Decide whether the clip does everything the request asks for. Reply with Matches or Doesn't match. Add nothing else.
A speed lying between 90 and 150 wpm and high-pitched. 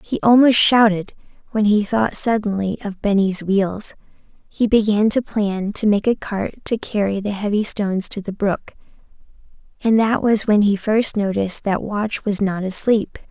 Doesn't match